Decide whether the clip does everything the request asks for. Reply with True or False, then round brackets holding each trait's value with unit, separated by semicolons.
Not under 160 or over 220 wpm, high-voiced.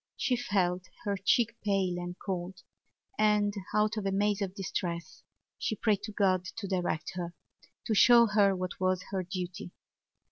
True (165 wpm; 195 Hz)